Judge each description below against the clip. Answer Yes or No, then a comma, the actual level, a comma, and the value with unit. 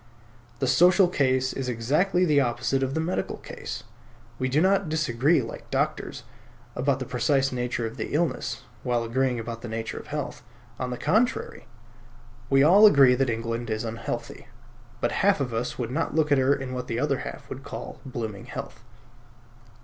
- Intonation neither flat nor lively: Yes, average, 3.9 semitones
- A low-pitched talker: Yes, low, 130 Hz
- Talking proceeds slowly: No, average, 180 wpm